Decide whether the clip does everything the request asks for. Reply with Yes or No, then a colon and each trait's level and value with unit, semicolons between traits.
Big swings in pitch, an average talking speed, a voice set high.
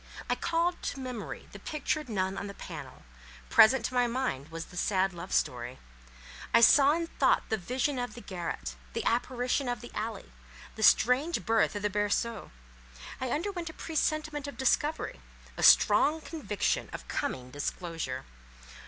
Yes: wide, 7.2 semitones; average, 165 wpm; high, 240 Hz